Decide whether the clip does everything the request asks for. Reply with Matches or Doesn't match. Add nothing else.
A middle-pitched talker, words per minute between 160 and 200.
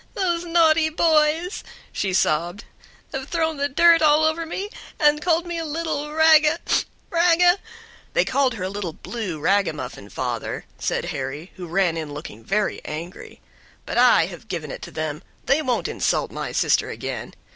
Doesn't match